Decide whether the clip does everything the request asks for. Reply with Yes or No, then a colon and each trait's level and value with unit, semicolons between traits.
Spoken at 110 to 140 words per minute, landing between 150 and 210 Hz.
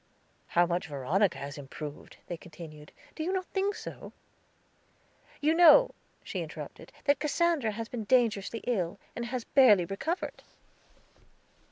No: slow, 135 wpm; high, 220 Hz